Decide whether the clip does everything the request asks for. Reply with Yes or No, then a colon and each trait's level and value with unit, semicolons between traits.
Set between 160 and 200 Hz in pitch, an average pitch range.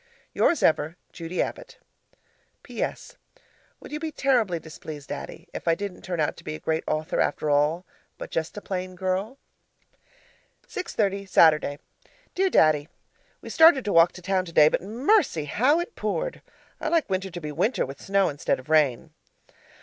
No: medium, 185 Hz; wide, 6.7 semitones